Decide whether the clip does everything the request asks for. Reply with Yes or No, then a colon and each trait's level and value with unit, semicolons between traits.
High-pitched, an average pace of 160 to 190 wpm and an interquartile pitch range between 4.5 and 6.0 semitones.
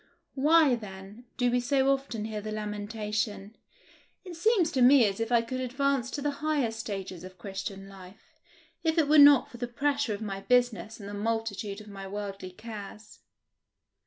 Yes: high, 225 Hz; average, 180 wpm; average, 4.9 semitones